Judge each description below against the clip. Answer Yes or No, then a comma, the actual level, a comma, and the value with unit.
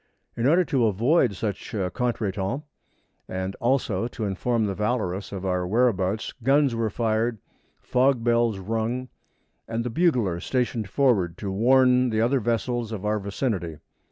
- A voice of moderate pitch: No, low, 115 Hz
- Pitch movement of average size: Yes, average, 3.9 semitones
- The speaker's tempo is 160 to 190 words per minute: No, average, 150 wpm